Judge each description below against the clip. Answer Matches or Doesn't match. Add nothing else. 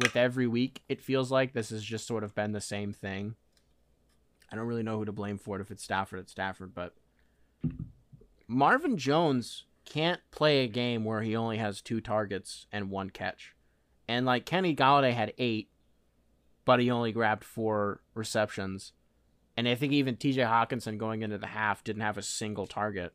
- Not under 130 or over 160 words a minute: Doesn't match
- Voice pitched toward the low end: Matches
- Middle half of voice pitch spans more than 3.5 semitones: Matches